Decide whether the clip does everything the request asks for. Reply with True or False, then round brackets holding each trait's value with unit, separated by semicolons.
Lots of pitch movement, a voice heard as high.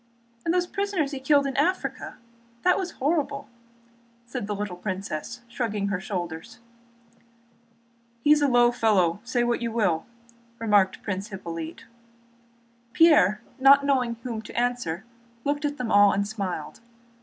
True (5.8 semitones; 235 Hz)